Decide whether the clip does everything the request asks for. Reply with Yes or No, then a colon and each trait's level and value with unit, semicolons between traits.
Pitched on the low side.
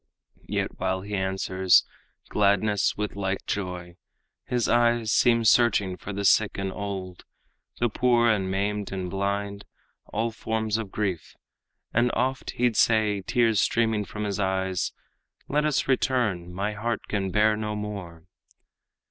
Yes: low, 105 Hz